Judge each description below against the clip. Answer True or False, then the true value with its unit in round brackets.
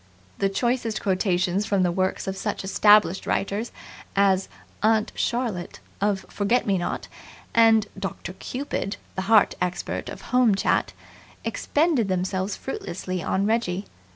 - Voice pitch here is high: True (200 Hz)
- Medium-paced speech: False (130 wpm)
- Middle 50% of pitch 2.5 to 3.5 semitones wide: True (3.0 semitones)